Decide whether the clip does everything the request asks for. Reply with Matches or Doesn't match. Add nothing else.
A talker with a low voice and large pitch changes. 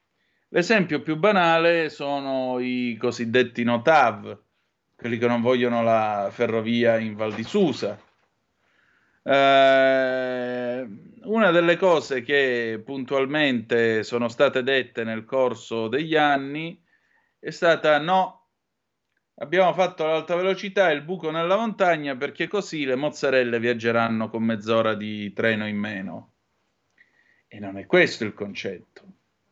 Matches